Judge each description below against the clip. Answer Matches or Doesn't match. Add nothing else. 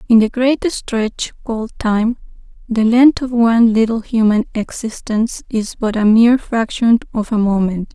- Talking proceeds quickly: Doesn't match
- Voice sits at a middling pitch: Doesn't match